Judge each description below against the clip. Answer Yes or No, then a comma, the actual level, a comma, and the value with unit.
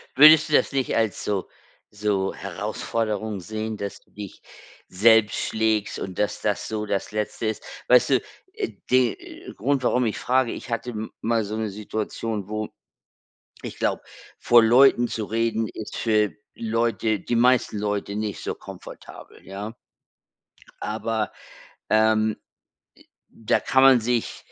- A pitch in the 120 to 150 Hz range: No, low, 110 Hz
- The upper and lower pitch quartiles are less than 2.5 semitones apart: Yes, narrow, 1.9 semitones